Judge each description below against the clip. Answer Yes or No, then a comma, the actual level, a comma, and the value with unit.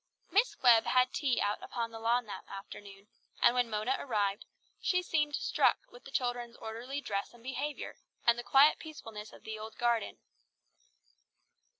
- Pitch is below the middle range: No, high, 240 Hz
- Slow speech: No, average, 165 wpm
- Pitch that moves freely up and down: No, average, 3.3 semitones